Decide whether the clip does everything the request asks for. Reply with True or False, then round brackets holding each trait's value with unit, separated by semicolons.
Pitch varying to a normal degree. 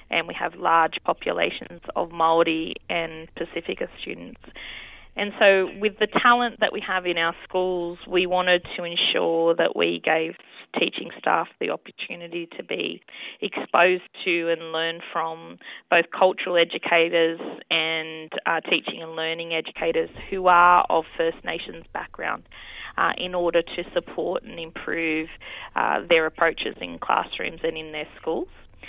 False (1.7 semitones)